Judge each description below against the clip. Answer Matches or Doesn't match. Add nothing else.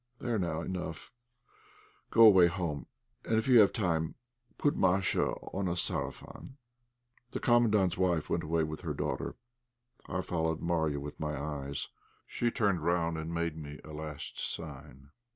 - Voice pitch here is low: Matches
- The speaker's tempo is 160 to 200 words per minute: Doesn't match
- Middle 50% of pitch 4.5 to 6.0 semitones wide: Doesn't match